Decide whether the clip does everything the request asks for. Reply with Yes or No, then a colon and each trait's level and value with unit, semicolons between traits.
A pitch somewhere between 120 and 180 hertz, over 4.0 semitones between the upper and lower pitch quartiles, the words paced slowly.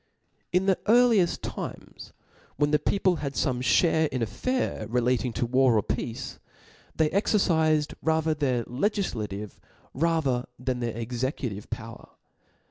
Yes: low, 135 Hz; average, 5.2 semitones; slow, 130 wpm